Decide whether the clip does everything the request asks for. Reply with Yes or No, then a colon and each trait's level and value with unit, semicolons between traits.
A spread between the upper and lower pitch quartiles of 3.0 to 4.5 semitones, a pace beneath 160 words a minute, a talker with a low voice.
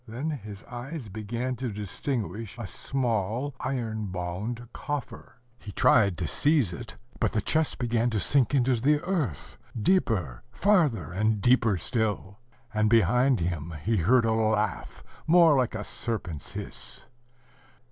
Yes: average, 4.0 semitones; average, 140 wpm; low, 115 Hz